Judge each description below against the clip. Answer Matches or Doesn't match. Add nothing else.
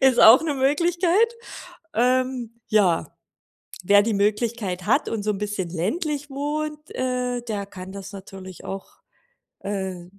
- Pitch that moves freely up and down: Matches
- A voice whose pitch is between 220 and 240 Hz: Matches